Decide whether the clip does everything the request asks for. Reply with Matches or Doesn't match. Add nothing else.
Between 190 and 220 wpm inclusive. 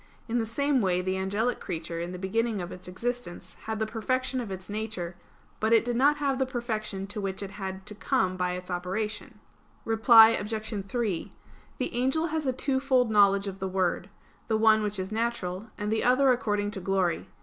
Matches